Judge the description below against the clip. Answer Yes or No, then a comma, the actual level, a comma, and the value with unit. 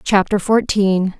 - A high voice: Yes, high, 200 Hz